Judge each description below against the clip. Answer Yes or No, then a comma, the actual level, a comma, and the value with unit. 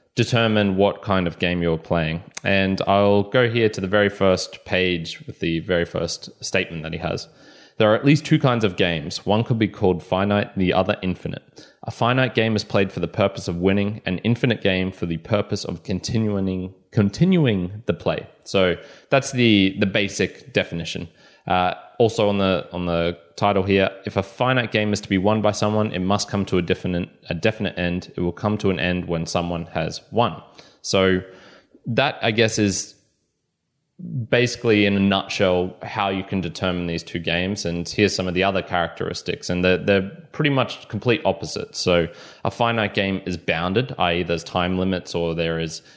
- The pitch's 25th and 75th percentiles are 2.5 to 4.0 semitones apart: Yes, average, 3.1 semitones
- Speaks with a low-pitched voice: Yes, very low, 95 Hz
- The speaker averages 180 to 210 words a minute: Yes, average, 190 wpm